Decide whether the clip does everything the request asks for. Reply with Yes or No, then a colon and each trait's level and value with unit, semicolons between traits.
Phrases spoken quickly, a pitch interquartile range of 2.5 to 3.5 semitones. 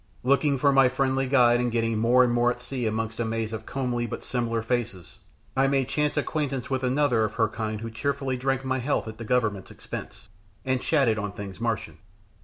Yes: fast, 210 wpm; average, 2.9 semitones